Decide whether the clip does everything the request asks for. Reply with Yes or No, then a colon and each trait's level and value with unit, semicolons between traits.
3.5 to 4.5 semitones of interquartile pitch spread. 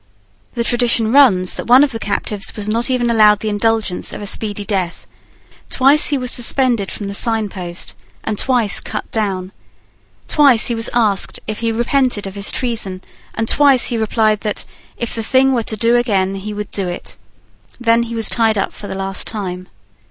No: average, 2.9 semitones